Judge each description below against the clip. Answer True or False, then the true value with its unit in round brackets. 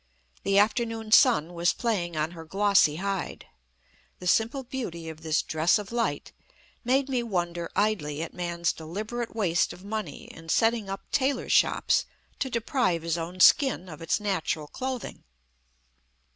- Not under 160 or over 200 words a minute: False (150 wpm)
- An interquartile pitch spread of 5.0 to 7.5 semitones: True (5.5 semitones)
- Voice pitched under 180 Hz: False (195 Hz)